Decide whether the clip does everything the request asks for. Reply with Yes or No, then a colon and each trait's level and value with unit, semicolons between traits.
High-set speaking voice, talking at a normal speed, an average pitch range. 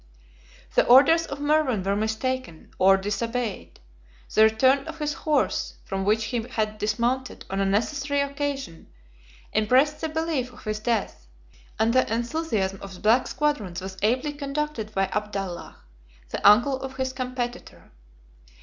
Yes: high, 240 Hz; average, 145 wpm; average, 4.9 semitones